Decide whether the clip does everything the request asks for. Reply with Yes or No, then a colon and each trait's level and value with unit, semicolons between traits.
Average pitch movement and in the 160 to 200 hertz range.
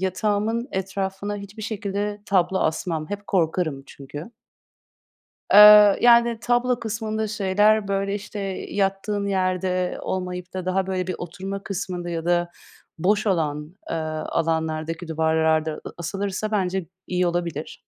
Yes: average, 3.0 semitones; high, 190 Hz